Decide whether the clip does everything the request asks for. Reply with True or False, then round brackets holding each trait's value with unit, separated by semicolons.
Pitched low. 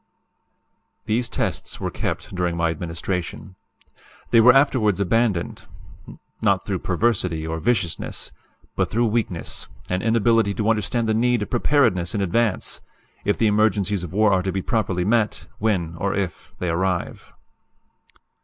True (100 Hz)